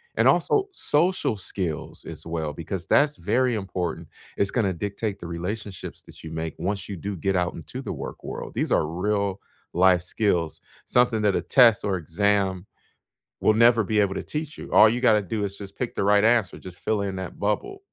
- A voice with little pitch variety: No, average, 3.7 semitones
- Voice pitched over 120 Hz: No, low, 100 Hz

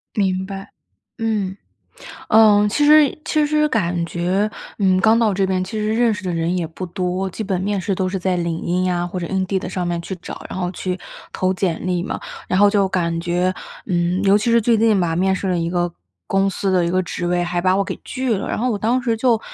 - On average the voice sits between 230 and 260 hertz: No, high, 190 Hz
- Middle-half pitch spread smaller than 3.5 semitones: Yes, average, 2.9 semitones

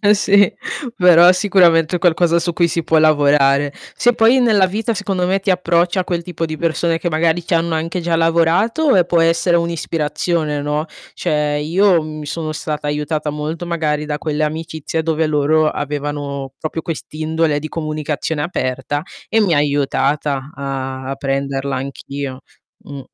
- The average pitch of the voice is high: No, medium, 160 Hz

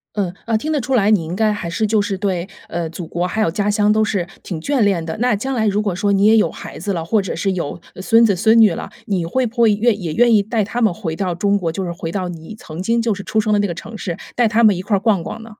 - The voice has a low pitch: No, high, 205 Hz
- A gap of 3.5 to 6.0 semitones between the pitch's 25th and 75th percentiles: Yes, average, 3.8 semitones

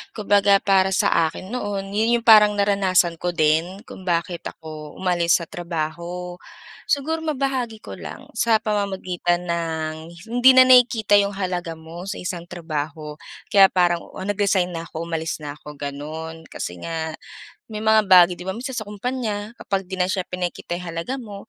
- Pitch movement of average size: Yes, average, 3.7 semitones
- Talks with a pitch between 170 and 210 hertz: Yes, medium, 185 Hz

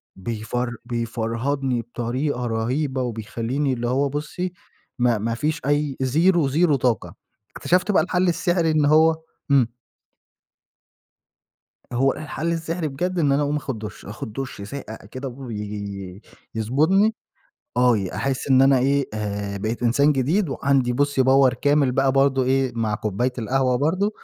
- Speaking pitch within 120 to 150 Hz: Yes, low, 135 Hz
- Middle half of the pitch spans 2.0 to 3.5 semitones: No, average, 4.0 semitones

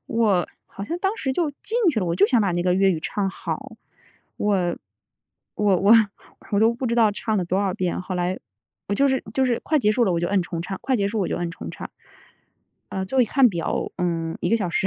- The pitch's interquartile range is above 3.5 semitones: Yes, average, 4.6 semitones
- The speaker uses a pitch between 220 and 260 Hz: No, high, 200 Hz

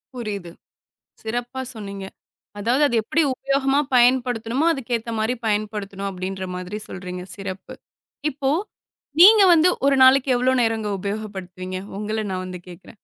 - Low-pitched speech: No, high, 220 Hz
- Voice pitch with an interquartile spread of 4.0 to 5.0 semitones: Yes, average, 4.7 semitones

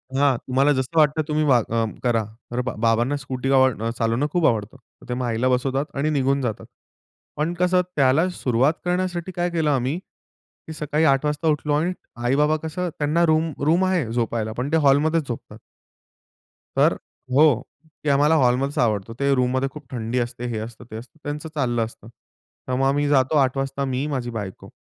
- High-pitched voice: No, low, 135 Hz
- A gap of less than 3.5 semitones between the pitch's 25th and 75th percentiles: No, average, 3.8 semitones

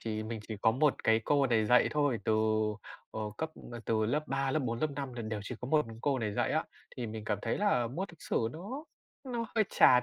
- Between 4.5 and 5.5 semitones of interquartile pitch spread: Yes, average, 5.1 semitones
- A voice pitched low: Yes, low, 125 Hz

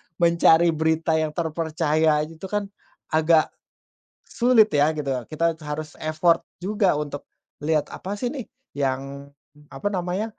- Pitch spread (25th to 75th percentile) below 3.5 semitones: Yes, average, 3.0 semitones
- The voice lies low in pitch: No, medium, 160 Hz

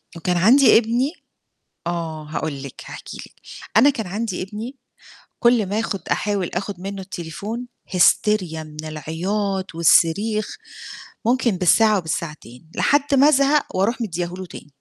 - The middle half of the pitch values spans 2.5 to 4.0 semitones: No, average, 5.3 semitones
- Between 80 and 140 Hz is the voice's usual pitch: No, high, 195 Hz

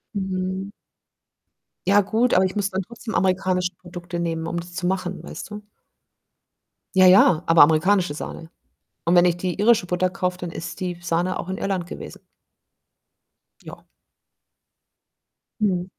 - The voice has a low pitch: No, medium, 185 Hz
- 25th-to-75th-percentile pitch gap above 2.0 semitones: No, narrow, 1.5 semitones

